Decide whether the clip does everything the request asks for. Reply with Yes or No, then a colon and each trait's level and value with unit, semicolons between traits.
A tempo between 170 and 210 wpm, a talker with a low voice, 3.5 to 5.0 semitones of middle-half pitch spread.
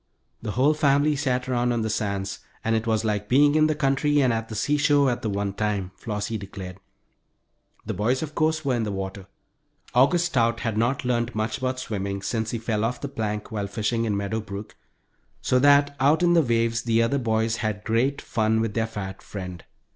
Yes: fast, 205 wpm; low, 115 Hz; average, 4.2 semitones